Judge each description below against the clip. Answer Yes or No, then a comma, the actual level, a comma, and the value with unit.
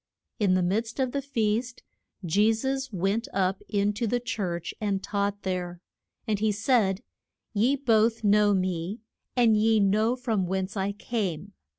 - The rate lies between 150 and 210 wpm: Yes, average, 160 wpm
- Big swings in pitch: No, average, 3.0 semitones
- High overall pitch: Yes, high, 210 Hz